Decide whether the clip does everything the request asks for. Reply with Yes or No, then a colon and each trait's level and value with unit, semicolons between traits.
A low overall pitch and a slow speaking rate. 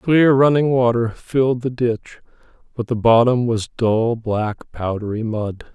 No: low, 120 Hz; average, 145 wpm